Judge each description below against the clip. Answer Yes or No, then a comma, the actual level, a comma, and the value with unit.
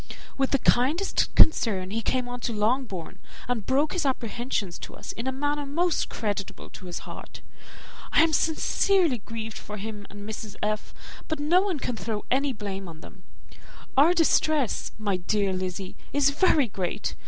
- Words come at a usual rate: Yes, average, 170 wpm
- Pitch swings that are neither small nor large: No, wide, 6.0 semitones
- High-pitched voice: Yes, high, 240 Hz